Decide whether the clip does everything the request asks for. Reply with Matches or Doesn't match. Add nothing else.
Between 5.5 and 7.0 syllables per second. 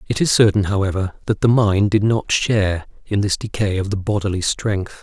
Doesn't match